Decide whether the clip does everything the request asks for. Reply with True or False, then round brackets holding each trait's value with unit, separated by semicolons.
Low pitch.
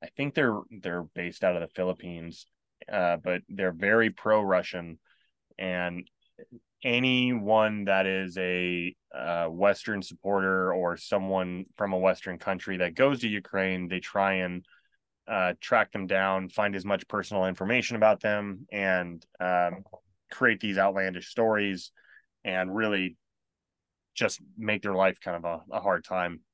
True (95 Hz)